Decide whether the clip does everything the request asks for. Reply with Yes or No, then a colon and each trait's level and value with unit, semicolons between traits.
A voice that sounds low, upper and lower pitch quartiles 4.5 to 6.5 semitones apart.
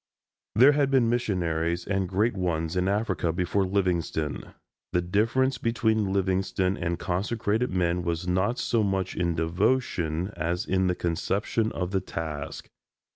No: very low, 95 Hz; average, 3.8 semitones